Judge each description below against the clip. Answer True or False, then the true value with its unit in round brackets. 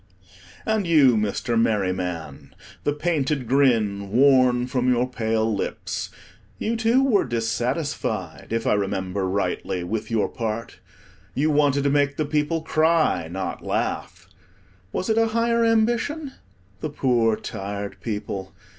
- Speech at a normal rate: False (130 wpm)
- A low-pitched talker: True (125 Hz)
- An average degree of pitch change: False (6.8 semitones)